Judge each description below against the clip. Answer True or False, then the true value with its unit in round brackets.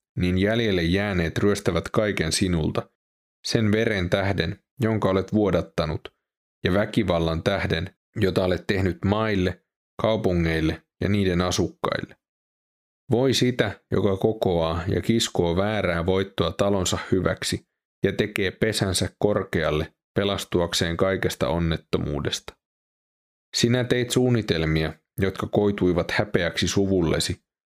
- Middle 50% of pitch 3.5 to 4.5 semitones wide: True (4.0 semitones)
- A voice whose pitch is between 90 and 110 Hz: True (95 Hz)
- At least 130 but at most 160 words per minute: False (100 wpm)